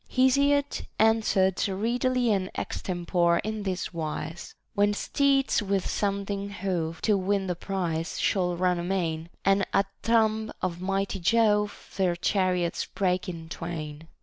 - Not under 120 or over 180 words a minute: Yes, average, 145 wpm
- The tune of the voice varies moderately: Yes, average, 3.3 semitones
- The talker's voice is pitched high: Yes, high, 195 Hz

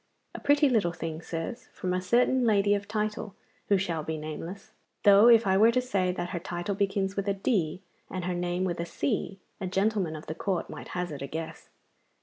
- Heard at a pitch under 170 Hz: No, high, 190 Hz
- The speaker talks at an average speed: No, fast, 210 wpm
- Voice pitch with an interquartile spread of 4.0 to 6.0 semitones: No, average, 3.1 semitones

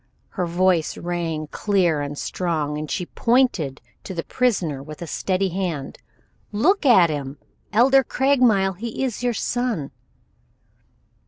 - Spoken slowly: Yes, slow, 130 wpm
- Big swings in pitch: Yes, wide, 7.1 semitones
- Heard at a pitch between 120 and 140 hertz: No, medium, 185 Hz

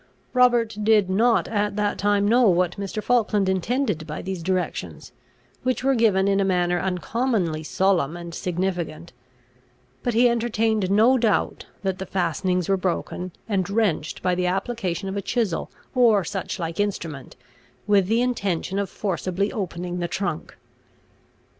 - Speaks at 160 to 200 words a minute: No, average, 150 wpm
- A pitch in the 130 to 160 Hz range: No, high, 195 Hz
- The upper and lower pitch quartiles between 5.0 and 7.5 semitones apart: No, average, 3.5 semitones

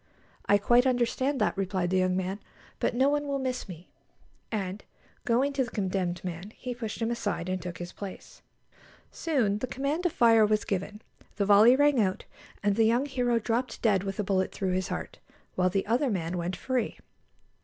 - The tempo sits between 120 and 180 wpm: No, average, 195 wpm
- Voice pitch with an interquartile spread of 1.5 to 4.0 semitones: No, average, 4.9 semitones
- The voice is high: Yes, high, 210 Hz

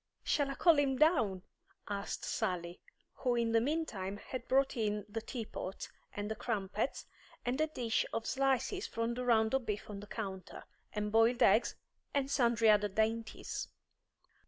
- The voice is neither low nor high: No, high, 230 Hz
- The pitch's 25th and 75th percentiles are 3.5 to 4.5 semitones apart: Yes, average, 4.0 semitones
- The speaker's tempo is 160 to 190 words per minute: Yes, average, 165 wpm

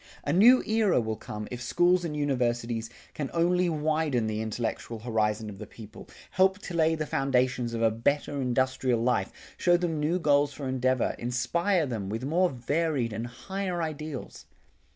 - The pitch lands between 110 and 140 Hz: Yes, low, 135 Hz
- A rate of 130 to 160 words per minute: No, average, 170 wpm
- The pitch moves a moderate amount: No, wide, 5.7 semitones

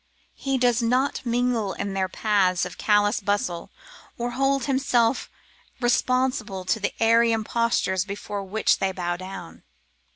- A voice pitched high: Yes, high, 220 Hz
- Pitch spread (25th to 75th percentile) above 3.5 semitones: Yes, average, 4.0 semitones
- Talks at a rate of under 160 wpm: Yes, slow, 135 wpm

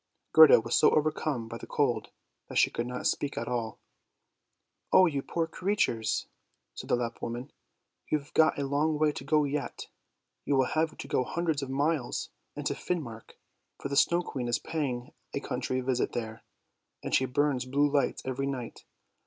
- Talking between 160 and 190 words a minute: Yes, average, 185 wpm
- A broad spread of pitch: No, average, 3.7 semitones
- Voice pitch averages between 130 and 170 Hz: Yes, medium, 140 Hz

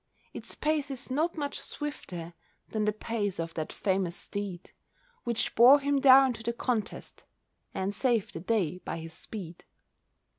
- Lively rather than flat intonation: Yes, wide, 6.5 semitones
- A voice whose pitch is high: Yes, high, 220 Hz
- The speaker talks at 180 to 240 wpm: No, average, 155 wpm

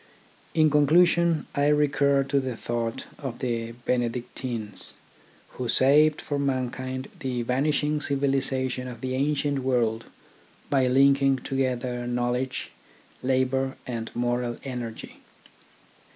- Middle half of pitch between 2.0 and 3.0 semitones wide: Yes, narrow, 2.4 semitones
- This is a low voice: Yes, low, 130 Hz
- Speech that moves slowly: Yes, slow, 110 wpm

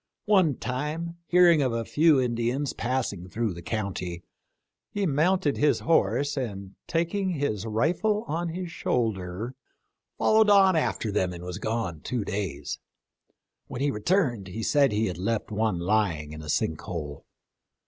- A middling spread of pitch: No, wide, 8.4 semitones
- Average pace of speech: Yes, average, 150 wpm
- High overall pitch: No, low, 120 Hz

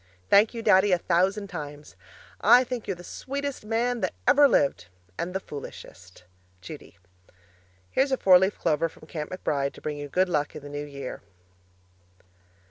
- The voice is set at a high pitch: No, medium, 180 Hz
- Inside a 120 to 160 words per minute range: No, average, 170 wpm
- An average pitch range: No, wide, 6.8 semitones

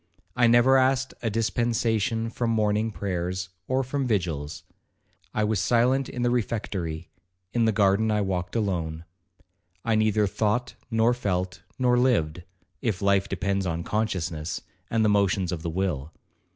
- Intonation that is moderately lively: Yes, average, 4.3 semitones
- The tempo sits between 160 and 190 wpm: No, average, 140 wpm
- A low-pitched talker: Yes, low, 105 Hz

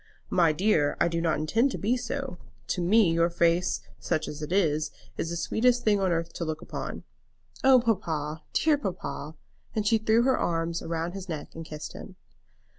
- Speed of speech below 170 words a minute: No, average, 190 wpm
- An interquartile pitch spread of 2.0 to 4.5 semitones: No, average, 5.1 semitones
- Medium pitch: Yes, medium, 170 Hz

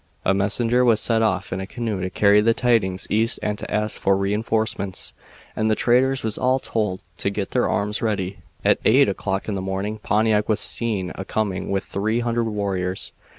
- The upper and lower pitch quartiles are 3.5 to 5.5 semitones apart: No, narrow, 2.6 semitones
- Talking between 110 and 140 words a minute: No, average, 200 wpm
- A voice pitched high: No, low, 105 Hz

